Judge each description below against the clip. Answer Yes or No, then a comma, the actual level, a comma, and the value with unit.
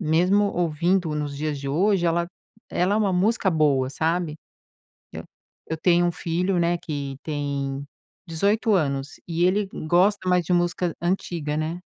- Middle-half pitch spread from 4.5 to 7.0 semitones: No, average, 3.2 semitones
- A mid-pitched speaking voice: Yes, medium, 170 Hz